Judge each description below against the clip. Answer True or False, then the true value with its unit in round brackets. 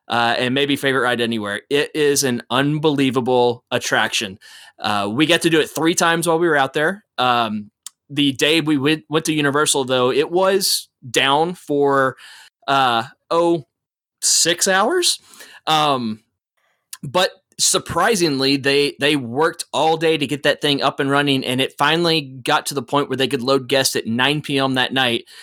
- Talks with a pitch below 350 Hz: True (140 Hz)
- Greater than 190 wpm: False (170 wpm)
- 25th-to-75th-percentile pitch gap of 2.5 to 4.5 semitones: True (3.1 semitones)